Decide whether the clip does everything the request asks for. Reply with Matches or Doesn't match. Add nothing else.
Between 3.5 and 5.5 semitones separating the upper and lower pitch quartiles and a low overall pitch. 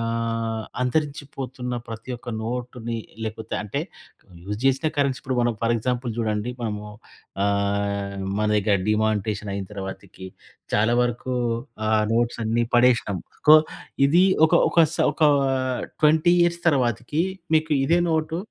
Matches